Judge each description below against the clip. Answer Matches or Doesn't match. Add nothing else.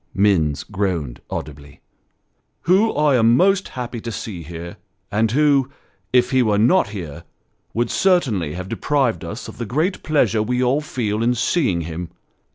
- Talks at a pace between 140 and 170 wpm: Matches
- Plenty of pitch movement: Matches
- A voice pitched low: Matches